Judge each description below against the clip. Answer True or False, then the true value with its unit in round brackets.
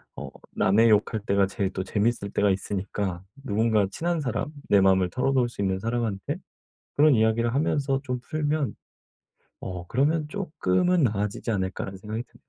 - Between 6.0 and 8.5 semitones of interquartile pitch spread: False (5.6 semitones)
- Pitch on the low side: True (110 Hz)